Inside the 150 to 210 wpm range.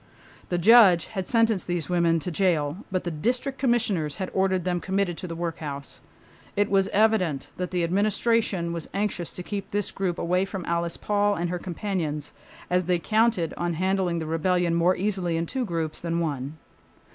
Yes: average, 185 wpm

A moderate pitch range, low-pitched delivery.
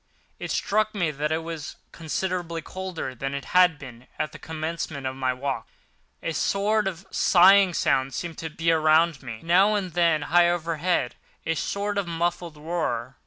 No: average, 3.3 semitones; medium, 165 Hz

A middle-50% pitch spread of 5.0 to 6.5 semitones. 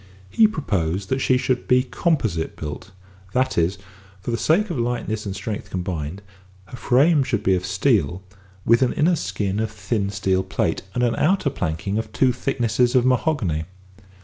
Yes: average, 5.3 semitones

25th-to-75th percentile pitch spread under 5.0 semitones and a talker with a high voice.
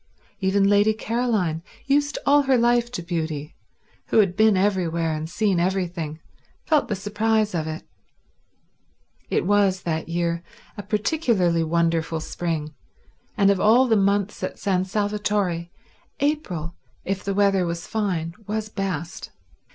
Yes: average, 4.0 semitones; high, 195 Hz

